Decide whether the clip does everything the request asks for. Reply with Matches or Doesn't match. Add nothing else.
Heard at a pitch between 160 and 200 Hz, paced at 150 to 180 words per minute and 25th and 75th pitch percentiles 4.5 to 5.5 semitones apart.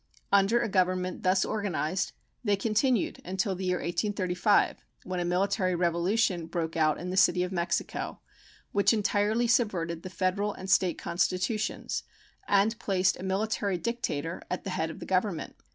Doesn't match